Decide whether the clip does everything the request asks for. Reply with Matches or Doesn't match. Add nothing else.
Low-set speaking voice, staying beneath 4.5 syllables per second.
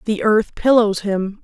Doesn't match